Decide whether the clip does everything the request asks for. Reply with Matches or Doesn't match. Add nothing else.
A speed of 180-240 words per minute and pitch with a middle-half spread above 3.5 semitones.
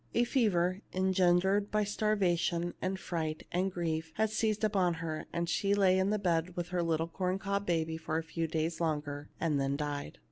Doesn't match